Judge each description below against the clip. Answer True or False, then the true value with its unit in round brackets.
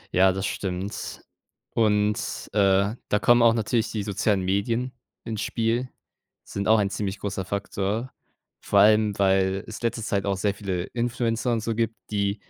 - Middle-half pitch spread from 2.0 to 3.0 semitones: True (2.6 semitones)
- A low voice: True (105 Hz)